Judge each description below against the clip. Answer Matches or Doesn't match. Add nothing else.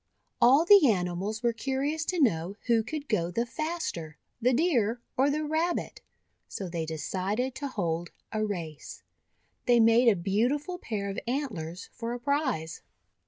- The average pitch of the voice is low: Doesn't match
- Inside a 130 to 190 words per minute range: Matches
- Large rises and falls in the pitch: Matches